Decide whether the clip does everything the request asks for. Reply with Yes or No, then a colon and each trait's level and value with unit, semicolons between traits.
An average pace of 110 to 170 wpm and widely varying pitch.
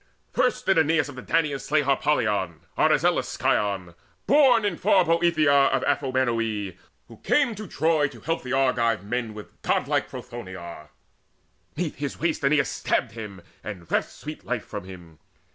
Yes: average, 150 wpm; wide, 7.2 semitones